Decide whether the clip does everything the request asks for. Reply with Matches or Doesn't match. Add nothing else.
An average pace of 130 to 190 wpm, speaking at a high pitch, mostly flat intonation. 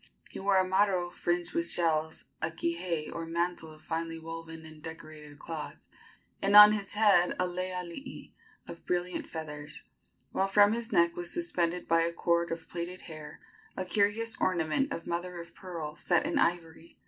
Doesn't match